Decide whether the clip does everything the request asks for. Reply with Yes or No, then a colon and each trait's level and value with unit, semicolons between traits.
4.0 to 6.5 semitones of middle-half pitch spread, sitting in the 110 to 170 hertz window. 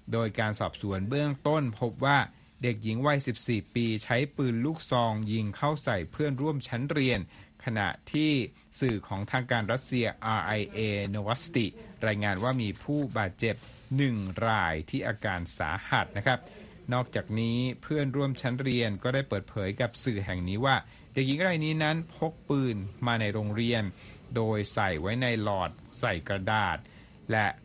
Yes: average, 4.4 semitones; low, 115 Hz